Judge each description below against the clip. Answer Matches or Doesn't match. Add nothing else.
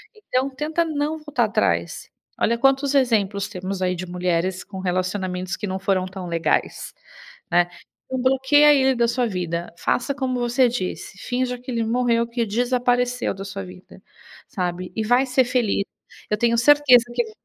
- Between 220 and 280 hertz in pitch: Matches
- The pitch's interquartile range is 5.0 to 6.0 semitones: Matches